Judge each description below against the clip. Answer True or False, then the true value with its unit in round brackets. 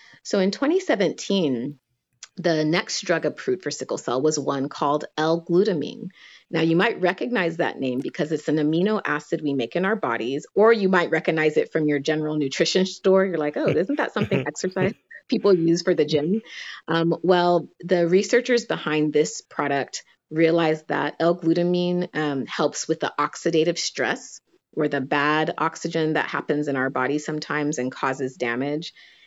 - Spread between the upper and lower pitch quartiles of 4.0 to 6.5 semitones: False (3.2 semitones)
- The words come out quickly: False (165 wpm)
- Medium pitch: True (160 Hz)